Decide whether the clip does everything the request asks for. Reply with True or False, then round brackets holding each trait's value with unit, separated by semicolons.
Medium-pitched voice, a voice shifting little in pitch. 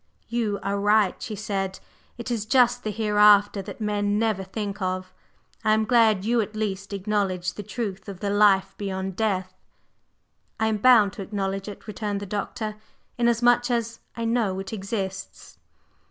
False (210 Hz; 2.3 semitones)